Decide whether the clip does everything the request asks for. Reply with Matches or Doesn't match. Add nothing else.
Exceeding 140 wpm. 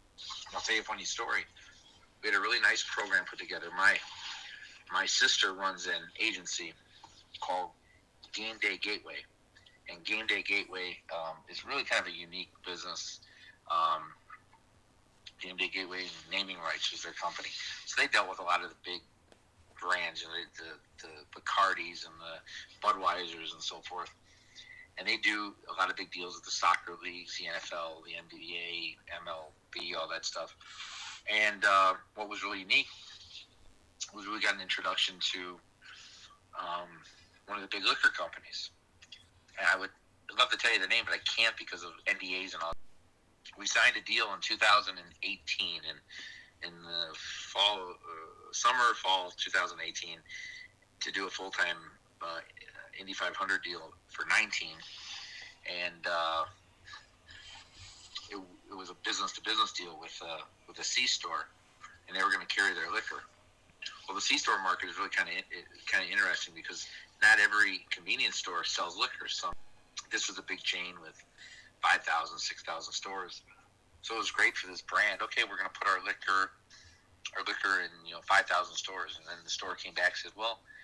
Matches